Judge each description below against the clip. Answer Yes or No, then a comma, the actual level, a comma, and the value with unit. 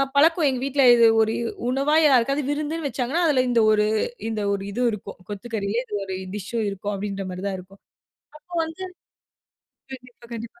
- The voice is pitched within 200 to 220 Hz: No, high, 240 Hz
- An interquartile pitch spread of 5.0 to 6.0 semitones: Yes, average, 5.3 semitones